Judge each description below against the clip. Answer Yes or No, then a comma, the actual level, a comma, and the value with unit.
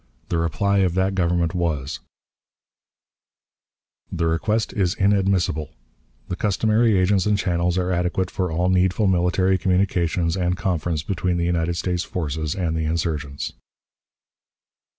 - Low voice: Yes, very low, 90 Hz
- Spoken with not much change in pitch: Yes, narrow, 2.2 semitones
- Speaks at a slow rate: Yes, slow, 130 wpm